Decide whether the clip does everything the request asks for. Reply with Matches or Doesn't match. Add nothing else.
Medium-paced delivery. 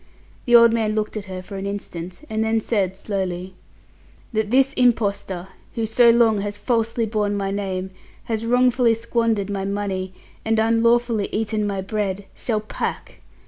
Matches